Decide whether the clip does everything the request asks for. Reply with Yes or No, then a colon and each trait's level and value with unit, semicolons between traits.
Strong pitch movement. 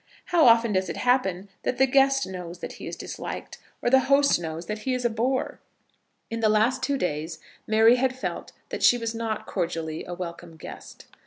Yes: wide, 6.3 semitones